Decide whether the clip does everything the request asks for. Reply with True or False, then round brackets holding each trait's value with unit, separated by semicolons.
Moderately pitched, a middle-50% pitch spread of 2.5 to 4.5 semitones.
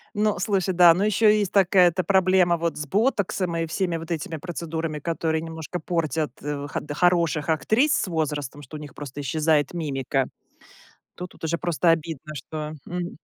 True (165 Hz; 2.9 semitones)